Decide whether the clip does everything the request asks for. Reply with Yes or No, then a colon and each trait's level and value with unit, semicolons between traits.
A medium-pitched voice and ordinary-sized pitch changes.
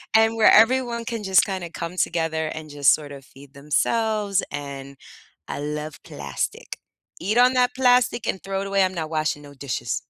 No: medium, 170 Hz; wide, 7.3 semitones